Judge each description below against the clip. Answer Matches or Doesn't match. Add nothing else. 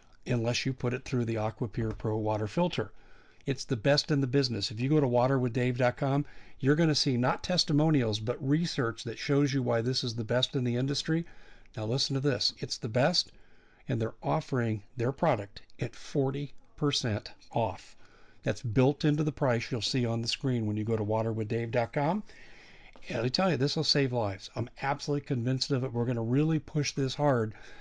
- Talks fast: Doesn't match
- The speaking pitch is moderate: Doesn't match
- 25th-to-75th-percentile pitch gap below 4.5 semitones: Matches